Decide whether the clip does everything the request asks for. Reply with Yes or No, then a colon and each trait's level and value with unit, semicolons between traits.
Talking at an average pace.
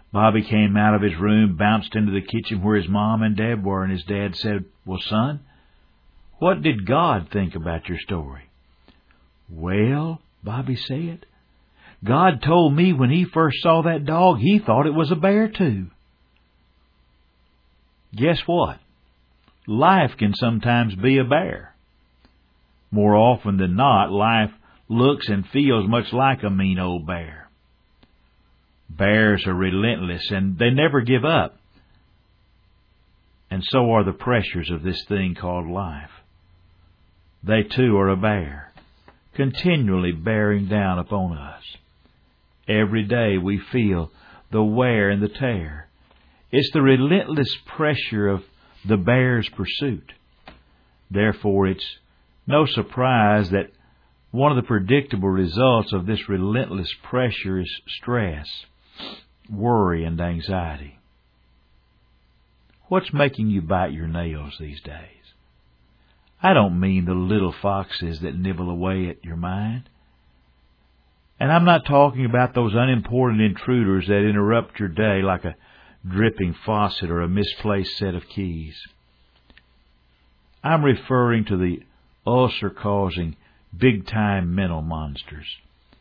No: slow, 130 wpm